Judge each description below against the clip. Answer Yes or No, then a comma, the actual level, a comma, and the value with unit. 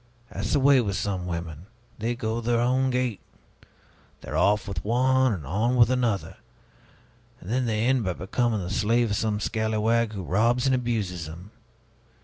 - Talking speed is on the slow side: No, average, 170 wpm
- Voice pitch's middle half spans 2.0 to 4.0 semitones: Yes, average, 3.6 semitones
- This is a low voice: Yes, low, 110 Hz